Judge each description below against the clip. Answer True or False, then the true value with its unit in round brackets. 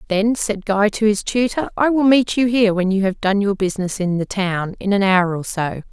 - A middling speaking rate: False (255 wpm)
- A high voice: True (205 Hz)